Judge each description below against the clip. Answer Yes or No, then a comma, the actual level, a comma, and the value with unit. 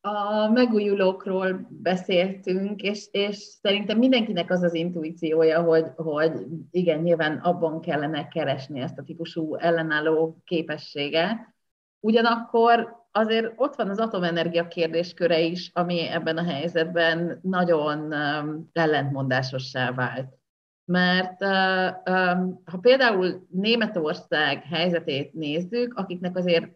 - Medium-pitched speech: Yes, medium, 175 Hz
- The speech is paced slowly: Yes, slow, 100 wpm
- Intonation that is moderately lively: Yes, average, 3.4 semitones